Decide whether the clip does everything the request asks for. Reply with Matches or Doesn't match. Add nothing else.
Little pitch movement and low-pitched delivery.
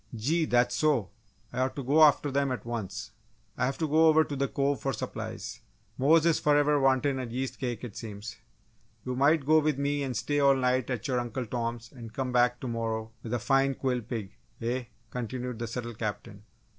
Doesn't match